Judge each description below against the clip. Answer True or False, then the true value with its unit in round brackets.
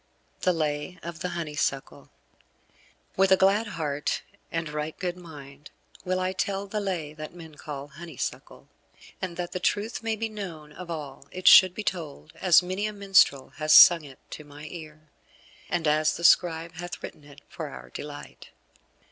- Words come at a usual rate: True (175 wpm)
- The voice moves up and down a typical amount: True (3.6 semitones)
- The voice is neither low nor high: True (165 Hz)